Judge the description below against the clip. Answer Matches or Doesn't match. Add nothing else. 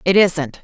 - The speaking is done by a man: Doesn't match